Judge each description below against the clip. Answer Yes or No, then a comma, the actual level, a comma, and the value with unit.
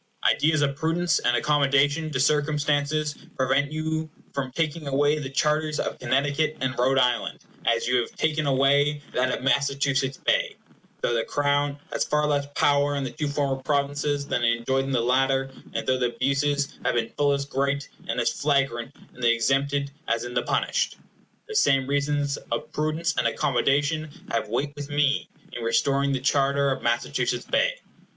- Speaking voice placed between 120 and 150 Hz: Yes, medium, 140 Hz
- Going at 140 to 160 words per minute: No, average, 175 wpm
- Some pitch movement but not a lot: No, narrow, 1.8 semitones